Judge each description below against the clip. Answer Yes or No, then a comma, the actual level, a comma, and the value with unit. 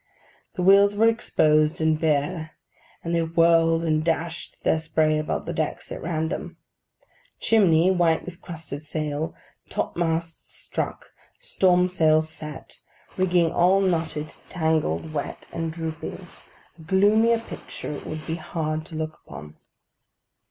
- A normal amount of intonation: No, narrow, 2.1 semitones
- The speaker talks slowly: Yes, slow, 130 wpm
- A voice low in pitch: No, medium, 165 Hz